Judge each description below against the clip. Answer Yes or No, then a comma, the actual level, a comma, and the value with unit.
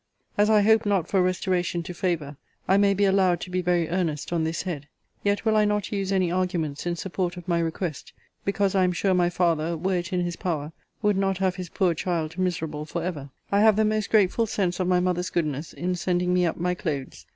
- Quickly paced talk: Yes, fast, 230 wpm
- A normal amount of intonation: No, narrow, 2.3 semitones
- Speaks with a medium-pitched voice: Yes, medium, 180 Hz